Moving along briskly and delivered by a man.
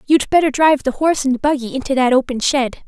No: fast, 230 wpm; female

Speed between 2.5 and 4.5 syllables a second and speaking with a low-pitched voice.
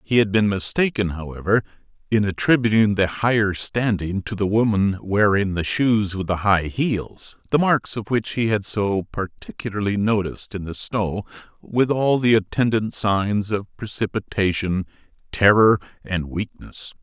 Yes: 4.4 syllables/s; low, 105 Hz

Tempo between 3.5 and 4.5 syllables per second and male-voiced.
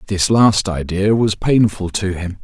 Yes: 4.1 syllables/s; male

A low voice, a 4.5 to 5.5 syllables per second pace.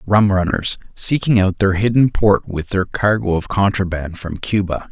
Yes: low, 100 Hz; 4.6 syllables/s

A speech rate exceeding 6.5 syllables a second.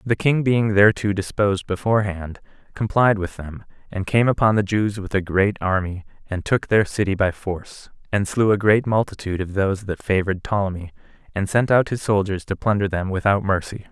No: 5.5 syllables/s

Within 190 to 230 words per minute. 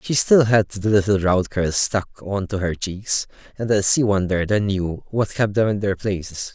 Yes: average, 200 wpm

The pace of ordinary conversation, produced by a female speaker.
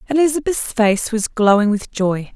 Yes: average, 155 wpm; female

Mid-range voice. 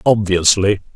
No: low, 100 Hz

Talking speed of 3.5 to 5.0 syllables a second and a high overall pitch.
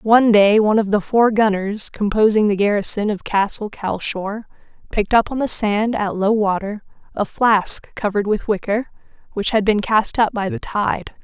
Yes: 4.8 syllables/s; high, 210 Hz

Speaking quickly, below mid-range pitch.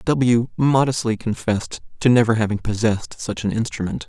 No: average, 145 wpm; low, 115 Hz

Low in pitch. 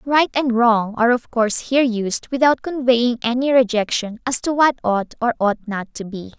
No: high, 240 Hz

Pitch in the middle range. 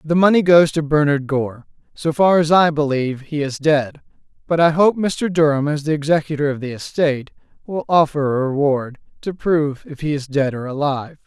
Yes: medium, 150 Hz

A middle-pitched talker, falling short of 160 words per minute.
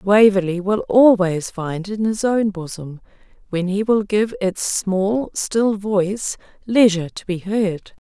No: high, 200 Hz; average, 150 wpm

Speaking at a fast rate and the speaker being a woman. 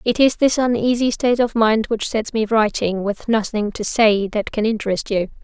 Yes: fast, 210 wpm; female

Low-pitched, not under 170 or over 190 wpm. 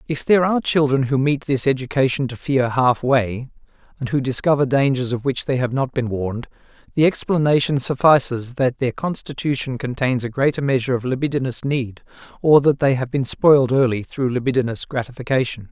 Yes: low, 130 Hz; average, 175 wpm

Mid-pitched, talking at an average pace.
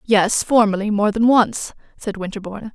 No: high, 210 Hz; average, 155 wpm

